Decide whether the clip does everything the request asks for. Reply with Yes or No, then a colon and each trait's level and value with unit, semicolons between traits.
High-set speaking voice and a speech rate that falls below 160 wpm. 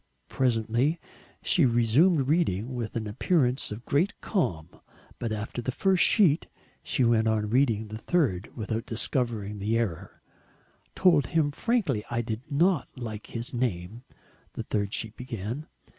No: low, 120 Hz; average, 145 wpm